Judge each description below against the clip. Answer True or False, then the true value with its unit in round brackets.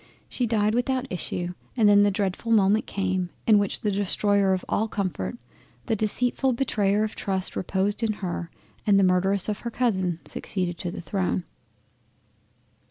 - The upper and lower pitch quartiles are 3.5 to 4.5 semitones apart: False (2.7 semitones)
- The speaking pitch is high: True (200 Hz)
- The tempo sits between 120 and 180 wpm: True (165 wpm)